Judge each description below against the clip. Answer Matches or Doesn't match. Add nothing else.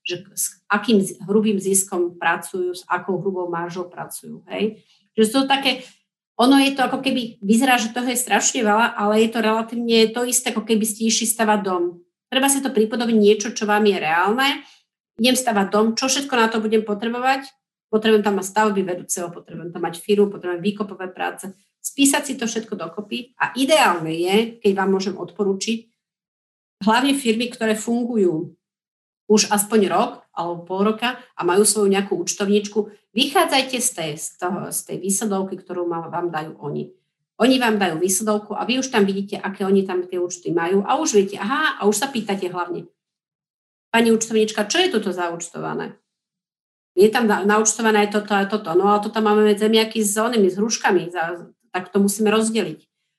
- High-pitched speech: Matches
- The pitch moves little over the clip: Doesn't match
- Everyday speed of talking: Doesn't match